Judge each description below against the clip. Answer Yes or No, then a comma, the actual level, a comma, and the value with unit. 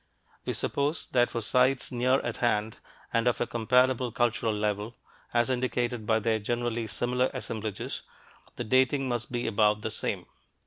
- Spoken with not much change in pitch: Yes, narrow, 2.2 semitones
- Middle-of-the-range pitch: No, low, 120 Hz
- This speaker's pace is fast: No, average, 160 wpm